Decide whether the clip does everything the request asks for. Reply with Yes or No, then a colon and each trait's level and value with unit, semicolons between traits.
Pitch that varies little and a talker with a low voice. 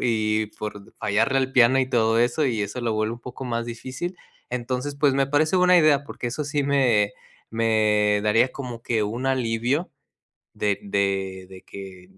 No: average, 3.8 semitones; low, 120 Hz